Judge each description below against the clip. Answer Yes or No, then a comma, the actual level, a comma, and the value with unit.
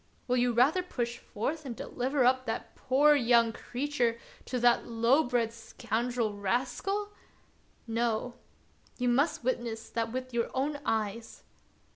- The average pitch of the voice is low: No, high, 245 Hz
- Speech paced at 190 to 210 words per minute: No, slow, 135 wpm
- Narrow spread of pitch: Yes, narrow, 2.3 semitones